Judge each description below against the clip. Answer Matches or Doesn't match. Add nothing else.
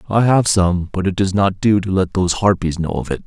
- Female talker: Doesn't match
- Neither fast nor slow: Doesn't match